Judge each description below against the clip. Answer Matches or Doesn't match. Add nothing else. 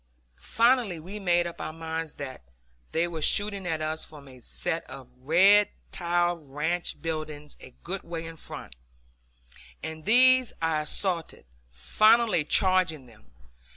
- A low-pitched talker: Doesn't match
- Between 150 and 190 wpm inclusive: Doesn't match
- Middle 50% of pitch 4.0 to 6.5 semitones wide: Doesn't match